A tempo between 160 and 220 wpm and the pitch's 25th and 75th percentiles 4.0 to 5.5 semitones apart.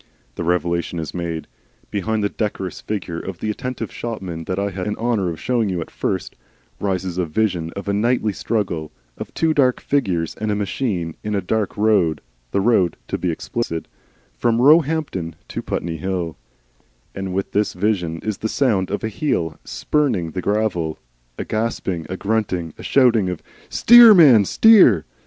Yes: average, 175 wpm; average, 4.4 semitones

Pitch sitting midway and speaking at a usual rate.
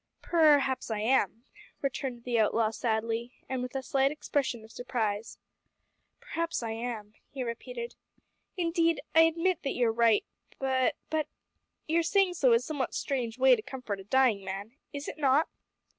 No: very high, 255 Hz; average, 165 wpm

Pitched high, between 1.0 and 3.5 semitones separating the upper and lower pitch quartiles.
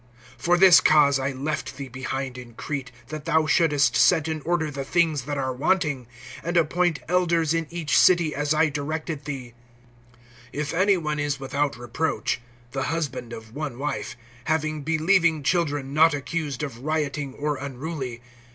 No: medium, 150 Hz; average, 2.9 semitones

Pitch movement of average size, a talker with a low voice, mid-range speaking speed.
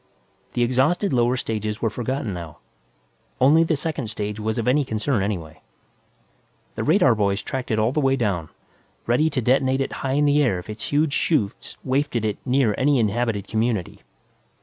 Yes: average, 4.2 semitones; low, 120 Hz; average, 175 wpm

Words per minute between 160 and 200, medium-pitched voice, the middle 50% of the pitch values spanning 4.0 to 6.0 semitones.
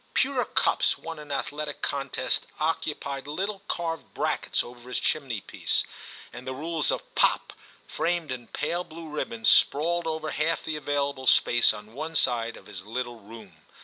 Yes: average, 175 wpm; medium, 145 Hz; average, 4.7 semitones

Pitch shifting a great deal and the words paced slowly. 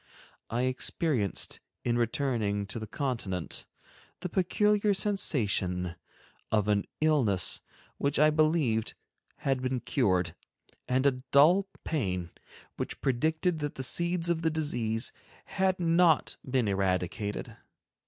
Yes: wide, 7.3 semitones; slow, 115 wpm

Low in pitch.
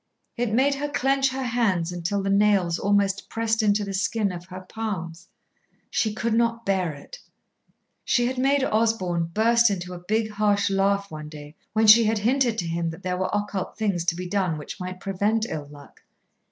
No: high, 200 Hz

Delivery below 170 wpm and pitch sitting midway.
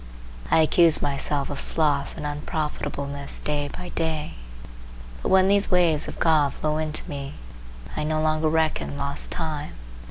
Yes: average, 150 wpm; medium, 155 Hz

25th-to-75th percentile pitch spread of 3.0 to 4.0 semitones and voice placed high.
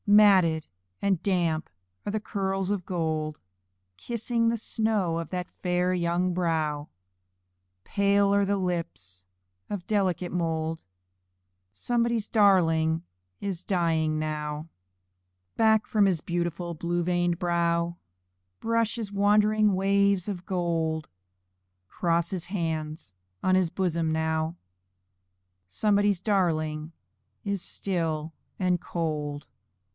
No: average, 3.7 semitones; medium, 175 Hz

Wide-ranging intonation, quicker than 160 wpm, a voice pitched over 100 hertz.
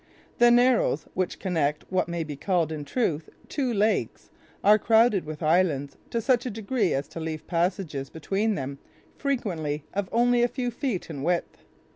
Yes: wide, 6.8 semitones; average, 170 wpm; medium, 185 Hz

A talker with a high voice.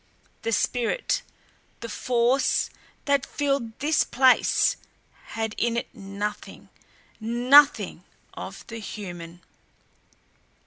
Yes: high, 235 Hz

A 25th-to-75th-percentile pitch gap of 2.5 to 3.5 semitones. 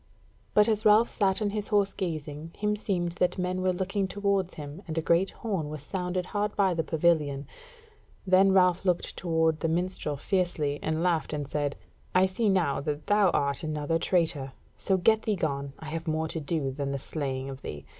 No: average, 4.2 semitones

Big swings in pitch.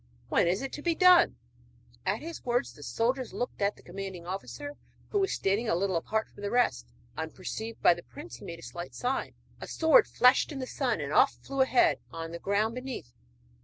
Yes: wide, 7.3 semitones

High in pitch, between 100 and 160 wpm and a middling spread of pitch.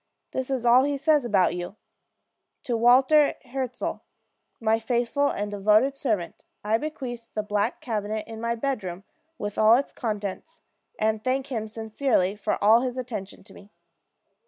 Yes: high, 230 Hz; average, 155 wpm; average, 3.7 semitones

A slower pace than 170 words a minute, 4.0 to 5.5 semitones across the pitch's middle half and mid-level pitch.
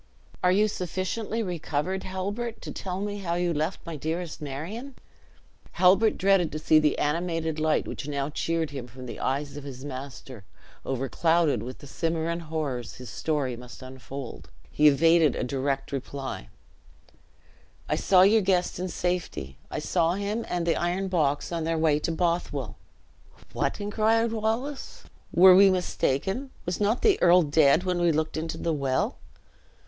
Yes: average, 160 wpm; average, 4.6 semitones; medium, 165 Hz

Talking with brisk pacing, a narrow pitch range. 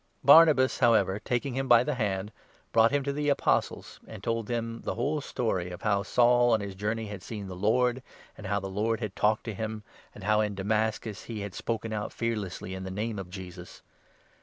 No: fast, 215 wpm; average, 3.0 semitones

